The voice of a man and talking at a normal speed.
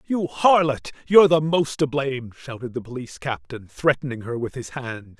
Yes: male; average, 185 wpm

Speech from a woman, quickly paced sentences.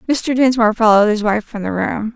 Yes: female; fast, 225 wpm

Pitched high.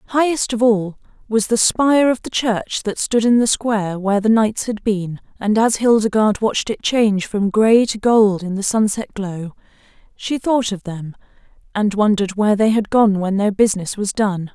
Yes: high, 215 Hz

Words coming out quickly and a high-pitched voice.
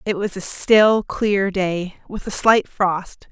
No: average, 180 wpm; high, 195 Hz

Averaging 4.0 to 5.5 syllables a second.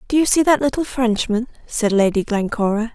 Yes: 5.4 syllables/s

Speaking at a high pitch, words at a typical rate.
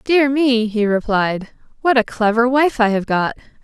Yes: high, 235 Hz; average, 180 wpm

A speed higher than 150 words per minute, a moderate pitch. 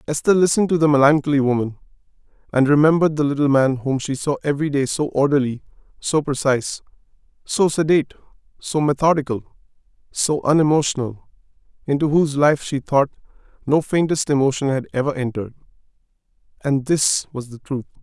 No: slow, 135 wpm; medium, 145 Hz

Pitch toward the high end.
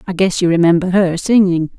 No: medium, 180 Hz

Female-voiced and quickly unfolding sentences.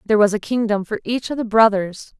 Yes: female; fast, 245 wpm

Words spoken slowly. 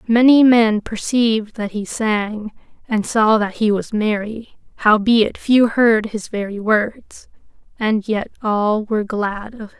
No: average, 155 wpm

